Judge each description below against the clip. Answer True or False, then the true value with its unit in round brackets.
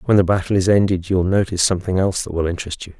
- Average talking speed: False (280 wpm)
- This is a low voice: True (95 Hz)